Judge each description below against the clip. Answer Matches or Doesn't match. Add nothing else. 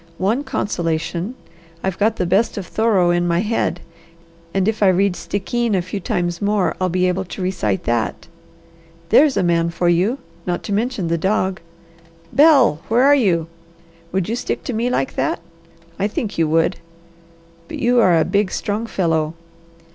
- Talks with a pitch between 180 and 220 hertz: Matches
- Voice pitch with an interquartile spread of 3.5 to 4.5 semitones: Matches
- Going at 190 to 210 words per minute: Doesn't match